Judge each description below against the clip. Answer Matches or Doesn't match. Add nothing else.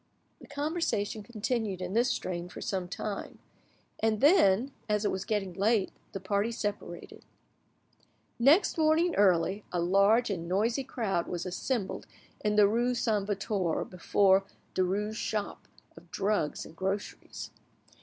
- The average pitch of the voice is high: Matches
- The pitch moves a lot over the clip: Doesn't match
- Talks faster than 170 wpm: Doesn't match